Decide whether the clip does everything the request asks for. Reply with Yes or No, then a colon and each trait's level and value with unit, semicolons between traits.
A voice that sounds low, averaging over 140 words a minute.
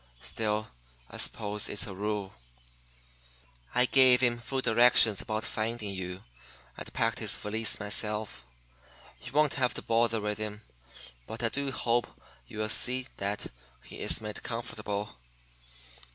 No: low, 110 Hz; slow, 135 wpm